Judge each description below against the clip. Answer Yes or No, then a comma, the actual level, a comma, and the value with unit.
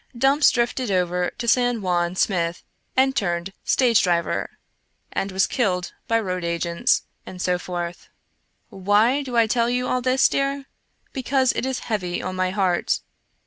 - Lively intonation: Yes, wide, 5.7 semitones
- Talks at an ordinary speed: Yes, average, 155 wpm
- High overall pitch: Yes, high, 205 Hz